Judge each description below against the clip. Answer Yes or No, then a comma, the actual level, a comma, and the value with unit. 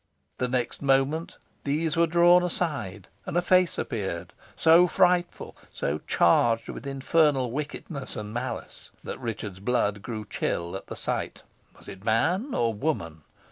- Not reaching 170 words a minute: Yes, average, 145 wpm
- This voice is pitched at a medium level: No, low, 130 Hz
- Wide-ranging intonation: Yes, wide, 7.5 semitones